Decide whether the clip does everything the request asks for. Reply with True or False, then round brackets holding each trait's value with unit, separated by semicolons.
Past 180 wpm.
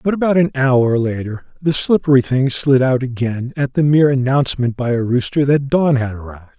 True (200 wpm)